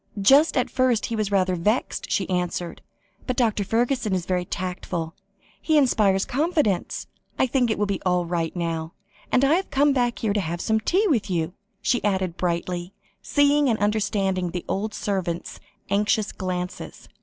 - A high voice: Yes, high, 200 Hz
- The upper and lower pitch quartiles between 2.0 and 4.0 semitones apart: No, wide, 5.4 semitones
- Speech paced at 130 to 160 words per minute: No, average, 170 wpm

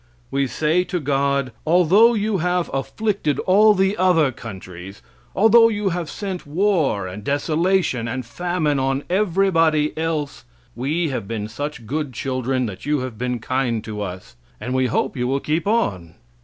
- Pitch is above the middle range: No, medium, 145 Hz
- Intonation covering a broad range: Yes, wide, 6.3 semitones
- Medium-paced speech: Yes, average, 160 wpm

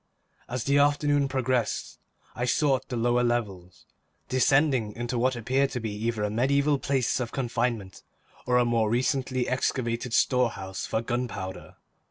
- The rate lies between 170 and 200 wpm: No, average, 145 wpm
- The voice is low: Yes, low, 125 Hz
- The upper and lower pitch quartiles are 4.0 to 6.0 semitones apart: No, narrow, 2.5 semitones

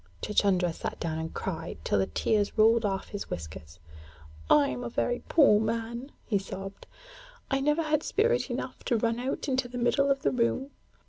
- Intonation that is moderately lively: No, wide, 6.1 semitones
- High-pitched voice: Yes, high, 225 Hz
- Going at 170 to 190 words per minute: Yes, average, 185 wpm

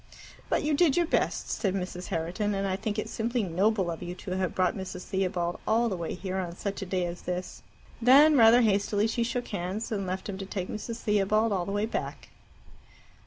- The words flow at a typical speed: No, fast, 215 wpm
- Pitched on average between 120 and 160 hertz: No, high, 195 Hz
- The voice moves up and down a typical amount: Yes, average, 3.4 semitones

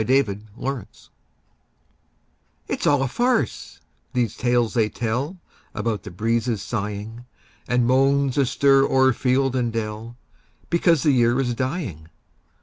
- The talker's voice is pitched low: Yes, low, 125 Hz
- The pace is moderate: No, slow, 125 wpm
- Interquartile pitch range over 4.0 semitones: No, average, 3.2 semitones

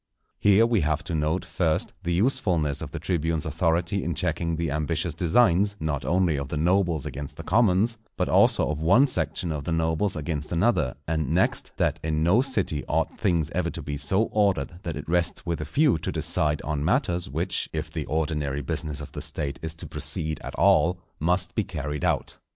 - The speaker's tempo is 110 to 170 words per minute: No, average, 200 wpm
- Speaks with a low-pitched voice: Yes, very low, 80 Hz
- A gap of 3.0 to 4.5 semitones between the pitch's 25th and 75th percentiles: Yes, average, 3.3 semitones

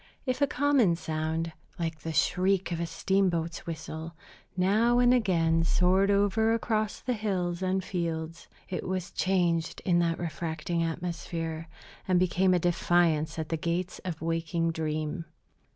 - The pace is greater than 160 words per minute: No, average, 145 wpm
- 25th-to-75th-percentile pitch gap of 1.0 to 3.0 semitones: Yes, narrow, 2.6 semitones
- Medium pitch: Yes, medium, 175 Hz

